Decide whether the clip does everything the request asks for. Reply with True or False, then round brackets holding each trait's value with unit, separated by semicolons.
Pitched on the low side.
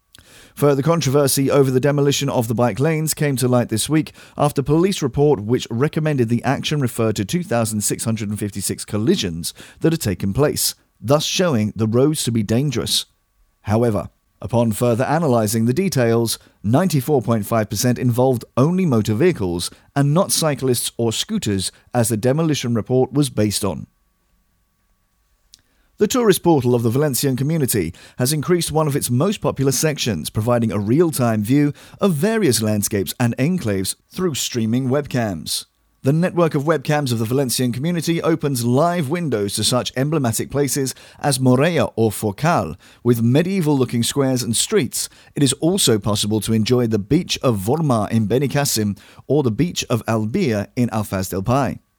True (125 Hz)